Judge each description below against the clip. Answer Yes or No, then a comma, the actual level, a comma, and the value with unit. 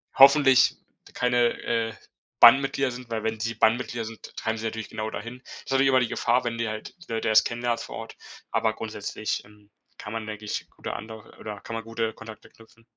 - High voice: No, low, 115 Hz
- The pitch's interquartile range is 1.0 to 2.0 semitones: Yes, narrow, 1.7 semitones